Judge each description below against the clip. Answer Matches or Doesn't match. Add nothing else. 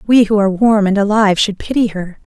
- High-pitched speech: Matches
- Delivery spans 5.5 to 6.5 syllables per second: Matches